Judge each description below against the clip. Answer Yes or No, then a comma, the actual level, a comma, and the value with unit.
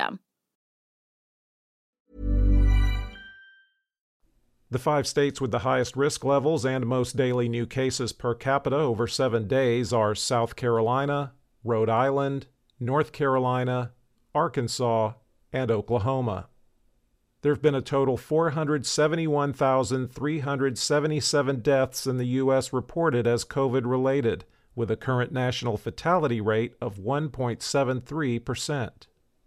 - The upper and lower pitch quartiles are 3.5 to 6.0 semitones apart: No, average, 2.9 semitones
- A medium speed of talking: No, slow, 100 wpm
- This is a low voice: Yes, low, 130 Hz